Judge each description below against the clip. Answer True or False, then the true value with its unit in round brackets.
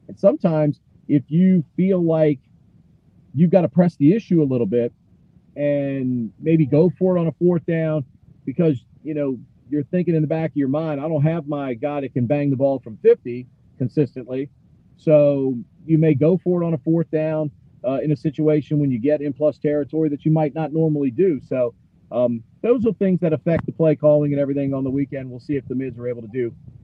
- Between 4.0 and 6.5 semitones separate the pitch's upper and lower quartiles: False (2.8 semitones)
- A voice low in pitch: False (150 Hz)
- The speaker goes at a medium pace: False (220 wpm)